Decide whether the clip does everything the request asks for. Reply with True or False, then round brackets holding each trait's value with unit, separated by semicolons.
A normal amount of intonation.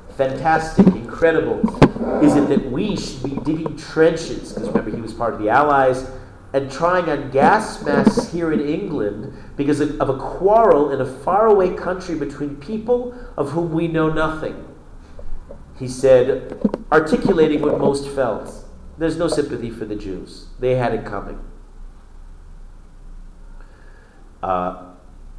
False (7.2 semitones)